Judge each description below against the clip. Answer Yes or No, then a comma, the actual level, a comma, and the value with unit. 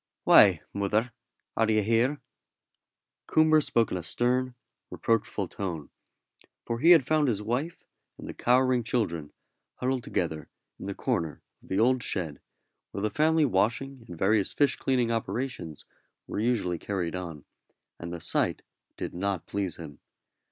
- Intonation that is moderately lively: No, wide, 5.8 semitones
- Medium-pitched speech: No, low, 110 Hz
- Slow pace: No, average, 150 wpm